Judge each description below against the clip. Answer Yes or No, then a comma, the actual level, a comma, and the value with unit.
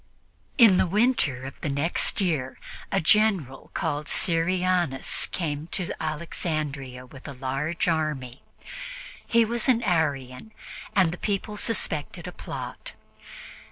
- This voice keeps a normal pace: No, slow, 120 wpm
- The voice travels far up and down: Yes, wide, 5.7 semitones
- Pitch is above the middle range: No, medium, 160 Hz